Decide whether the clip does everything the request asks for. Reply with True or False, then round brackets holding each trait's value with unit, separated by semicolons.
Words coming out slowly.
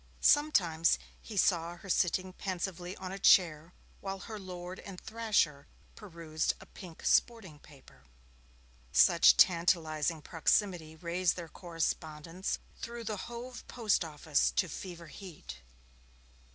True (120 wpm)